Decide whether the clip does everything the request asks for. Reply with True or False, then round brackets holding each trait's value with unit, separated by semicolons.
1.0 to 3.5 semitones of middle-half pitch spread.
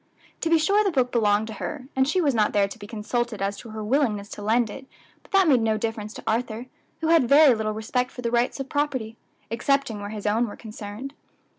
False (4.2 semitones)